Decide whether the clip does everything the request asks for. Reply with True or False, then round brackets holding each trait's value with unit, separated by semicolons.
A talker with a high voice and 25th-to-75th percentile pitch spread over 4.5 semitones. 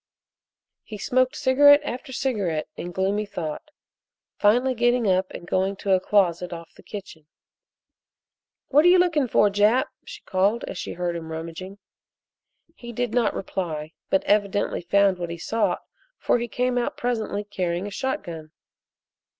True (205 Hz; 5.4 semitones)